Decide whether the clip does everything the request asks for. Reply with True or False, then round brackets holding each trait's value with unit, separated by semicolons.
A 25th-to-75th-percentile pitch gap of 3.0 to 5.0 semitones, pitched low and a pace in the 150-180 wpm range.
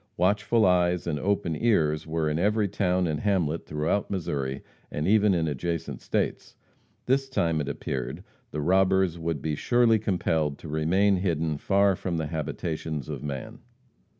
True (4.4 semitones; 85 Hz; 155 wpm)